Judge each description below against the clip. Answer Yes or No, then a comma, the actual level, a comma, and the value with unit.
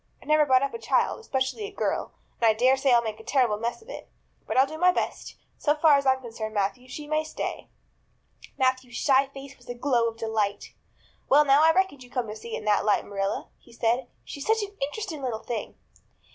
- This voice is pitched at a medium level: No, very high, 260 Hz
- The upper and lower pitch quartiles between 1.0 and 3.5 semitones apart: No, average, 4.2 semitones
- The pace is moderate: No, fast, 230 wpm